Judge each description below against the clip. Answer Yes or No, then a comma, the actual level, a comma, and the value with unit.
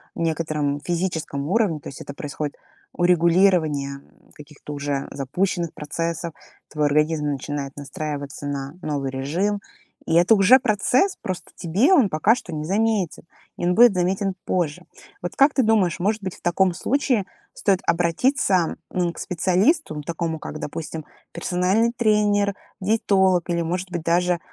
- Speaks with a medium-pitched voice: Yes, medium, 175 Hz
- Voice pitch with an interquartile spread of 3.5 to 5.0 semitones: Yes, average, 4.6 semitones